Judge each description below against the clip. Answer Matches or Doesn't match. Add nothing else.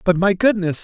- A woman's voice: Doesn't match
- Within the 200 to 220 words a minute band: Matches